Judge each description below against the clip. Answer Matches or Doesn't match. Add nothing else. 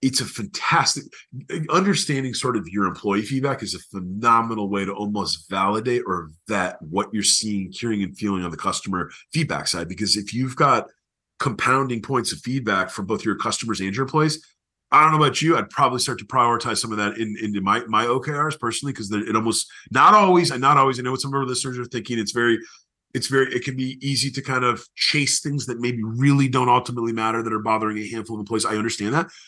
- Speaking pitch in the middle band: Doesn't match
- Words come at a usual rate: Doesn't match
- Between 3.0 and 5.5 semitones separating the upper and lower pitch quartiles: Matches